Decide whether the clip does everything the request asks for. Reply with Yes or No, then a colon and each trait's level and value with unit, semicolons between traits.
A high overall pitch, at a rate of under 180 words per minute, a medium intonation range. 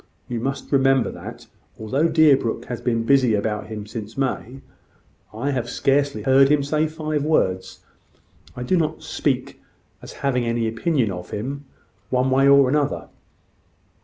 No: low, 130 Hz; average, 155 wpm; average, 3.6 semitones